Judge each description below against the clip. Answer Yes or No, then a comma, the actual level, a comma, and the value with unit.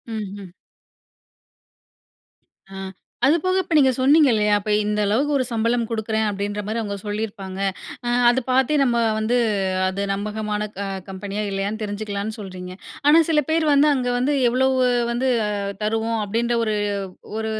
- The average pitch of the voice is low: No, high, 220 Hz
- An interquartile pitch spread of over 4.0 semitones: No, average, 3.7 semitones